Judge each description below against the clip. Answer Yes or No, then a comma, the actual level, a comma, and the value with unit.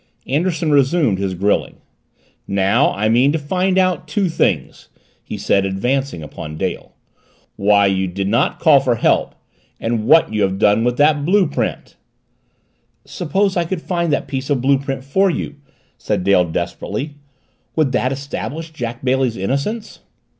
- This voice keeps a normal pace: Yes, average, 155 wpm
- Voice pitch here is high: No, low, 135 Hz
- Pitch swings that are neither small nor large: No, wide, 7.5 semitones